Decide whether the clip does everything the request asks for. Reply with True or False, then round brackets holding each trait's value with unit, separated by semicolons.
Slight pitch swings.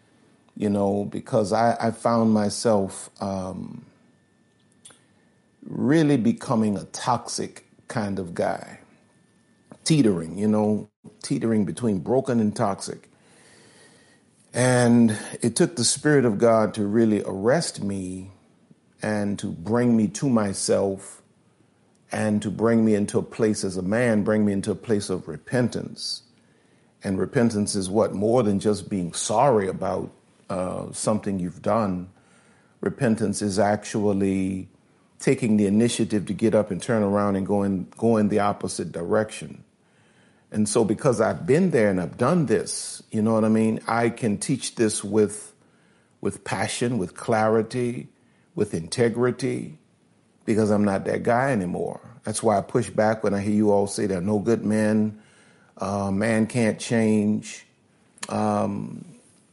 True (2.2 semitones)